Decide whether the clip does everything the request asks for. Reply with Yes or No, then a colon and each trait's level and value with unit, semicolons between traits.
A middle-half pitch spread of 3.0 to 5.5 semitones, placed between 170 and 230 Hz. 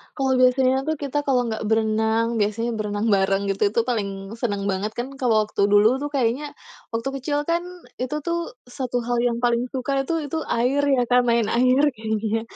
No: average, 3.5 semitones; high, 240 Hz